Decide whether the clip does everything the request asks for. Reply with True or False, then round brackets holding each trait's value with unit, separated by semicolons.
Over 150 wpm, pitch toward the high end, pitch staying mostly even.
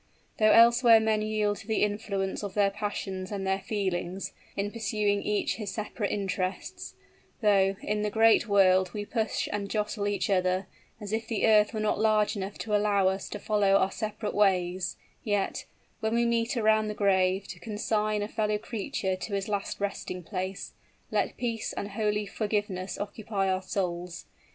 True (175 wpm; 205 Hz; 1.9 semitones)